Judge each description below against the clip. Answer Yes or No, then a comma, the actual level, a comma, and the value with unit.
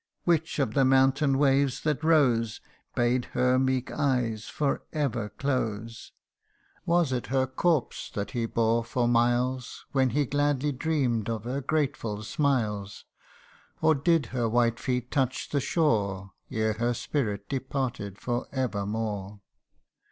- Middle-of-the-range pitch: No, low, 125 Hz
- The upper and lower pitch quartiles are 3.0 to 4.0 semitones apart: Yes, average, 3.6 semitones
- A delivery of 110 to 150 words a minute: Yes, slow, 135 wpm